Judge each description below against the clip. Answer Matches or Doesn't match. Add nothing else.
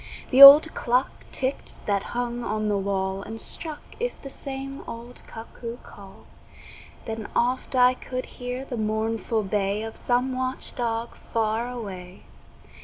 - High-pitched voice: Matches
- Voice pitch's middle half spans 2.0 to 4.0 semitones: Matches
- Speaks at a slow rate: Doesn't match